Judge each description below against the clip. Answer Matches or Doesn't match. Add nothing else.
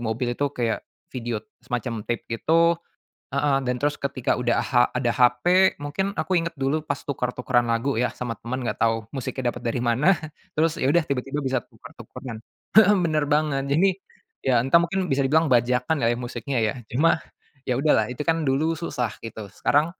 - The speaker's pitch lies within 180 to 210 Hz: Doesn't match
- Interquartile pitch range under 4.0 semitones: Doesn't match